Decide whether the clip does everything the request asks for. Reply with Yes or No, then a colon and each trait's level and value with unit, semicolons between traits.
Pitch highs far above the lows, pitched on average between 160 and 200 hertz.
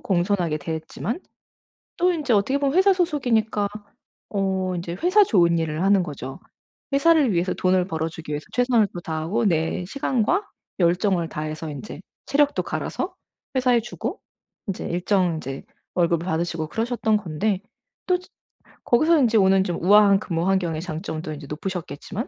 Yes: wide, 6.2 semitones; high, 190 Hz